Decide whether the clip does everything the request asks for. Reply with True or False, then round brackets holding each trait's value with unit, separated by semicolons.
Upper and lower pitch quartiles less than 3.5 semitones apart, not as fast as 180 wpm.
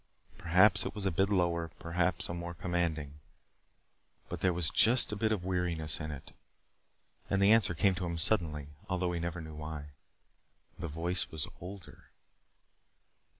True (2.7 semitones; 160 wpm)